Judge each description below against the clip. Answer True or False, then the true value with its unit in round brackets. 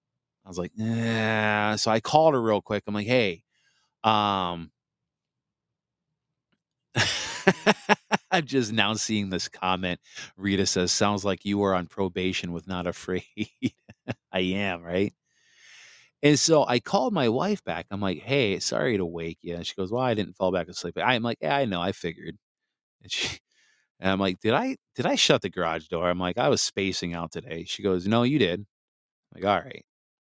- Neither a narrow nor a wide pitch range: True (4.3 semitones)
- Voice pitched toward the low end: True (100 Hz)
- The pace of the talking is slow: False (185 wpm)